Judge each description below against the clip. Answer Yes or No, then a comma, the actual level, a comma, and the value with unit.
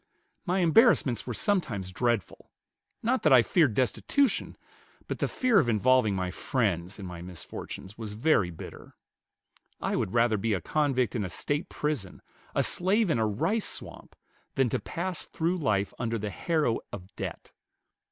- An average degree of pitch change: No, wide, 8.0 semitones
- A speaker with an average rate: Yes, average, 160 wpm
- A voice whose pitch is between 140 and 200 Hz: No, low, 120 Hz